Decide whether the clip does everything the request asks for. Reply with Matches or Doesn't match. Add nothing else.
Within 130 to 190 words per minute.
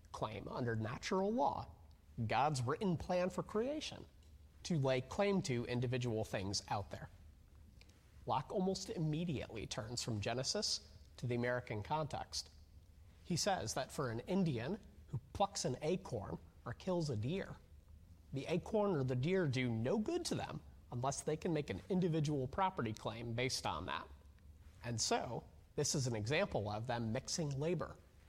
Matches